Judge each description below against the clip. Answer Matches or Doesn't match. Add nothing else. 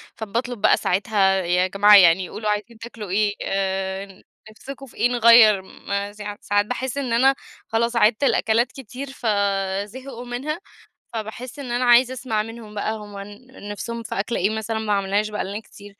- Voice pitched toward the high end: Matches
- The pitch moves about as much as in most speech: Matches